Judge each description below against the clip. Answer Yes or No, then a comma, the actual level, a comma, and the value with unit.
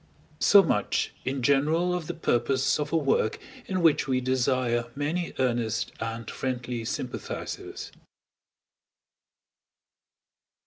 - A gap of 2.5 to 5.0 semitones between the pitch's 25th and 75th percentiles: Yes, average, 3.8 semitones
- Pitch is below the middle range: Yes, low, 130 Hz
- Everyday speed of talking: No, slow, 105 wpm